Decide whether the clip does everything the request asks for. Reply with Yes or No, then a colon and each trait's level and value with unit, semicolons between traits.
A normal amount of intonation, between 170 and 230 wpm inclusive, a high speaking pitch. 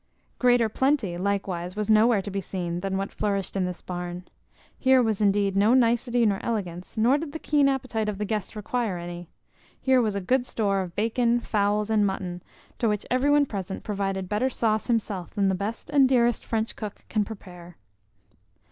Yes: average, 3.7 semitones; average, 185 wpm; high, 210 Hz